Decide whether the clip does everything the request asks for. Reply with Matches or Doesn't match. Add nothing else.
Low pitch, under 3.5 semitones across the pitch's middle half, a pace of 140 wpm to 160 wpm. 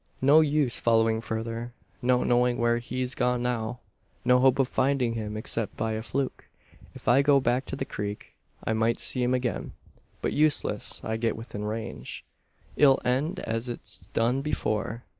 Doesn't match